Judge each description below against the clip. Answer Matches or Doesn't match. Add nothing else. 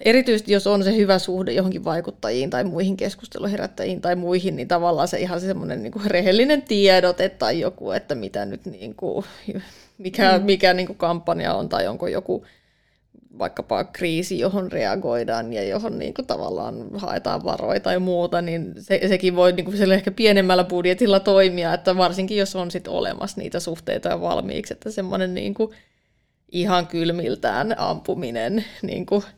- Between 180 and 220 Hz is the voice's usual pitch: Matches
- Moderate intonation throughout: Doesn't match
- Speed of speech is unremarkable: Doesn't match